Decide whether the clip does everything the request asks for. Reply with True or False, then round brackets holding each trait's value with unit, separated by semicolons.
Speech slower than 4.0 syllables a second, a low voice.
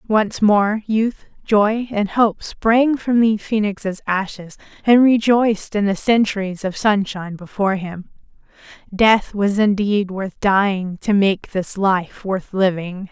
False (3.8 syllables/s; 205 Hz)